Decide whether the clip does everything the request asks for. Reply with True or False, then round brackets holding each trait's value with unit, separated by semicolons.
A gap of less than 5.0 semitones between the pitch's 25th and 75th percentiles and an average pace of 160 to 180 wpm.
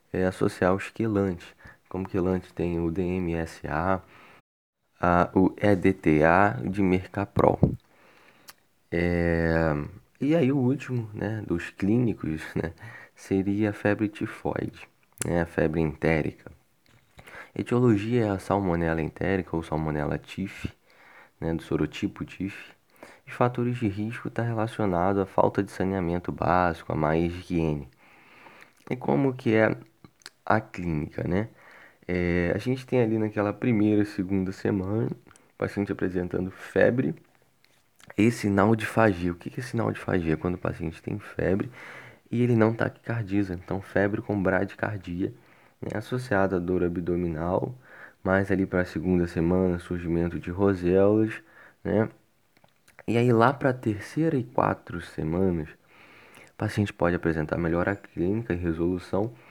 False (3.8 semitones; 135 wpm)